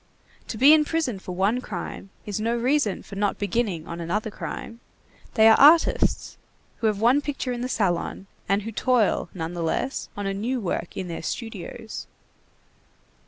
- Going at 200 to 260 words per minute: No, average, 165 wpm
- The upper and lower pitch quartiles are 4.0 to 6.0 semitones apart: Yes, average, 4.4 semitones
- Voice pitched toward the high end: Yes, high, 215 Hz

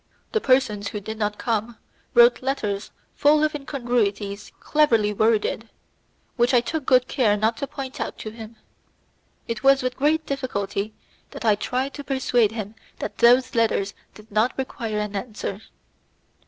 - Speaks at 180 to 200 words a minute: No, average, 155 wpm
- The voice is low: No, high, 230 Hz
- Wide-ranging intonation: No, average, 4.1 semitones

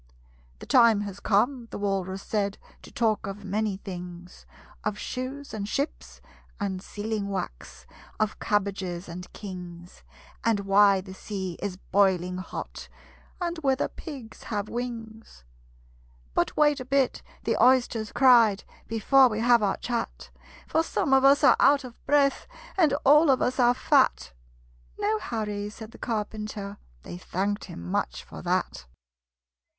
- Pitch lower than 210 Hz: No, high, 215 Hz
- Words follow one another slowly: No, average, 145 wpm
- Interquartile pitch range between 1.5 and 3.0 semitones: No, average, 4.4 semitones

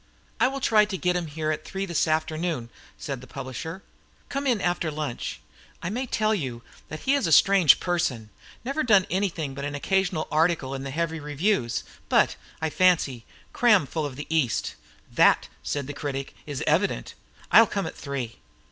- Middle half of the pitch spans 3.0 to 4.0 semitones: No, wide, 5.5 semitones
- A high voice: No, medium, 160 Hz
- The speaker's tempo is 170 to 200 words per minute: Yes, average, 185 wpm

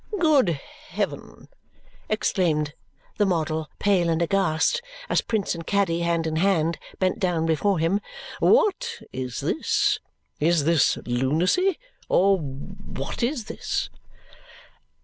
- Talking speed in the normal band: No, slow, 115 wpm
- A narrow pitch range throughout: No, average, 4.1 semitones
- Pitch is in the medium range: Yes, medium, 170 Hz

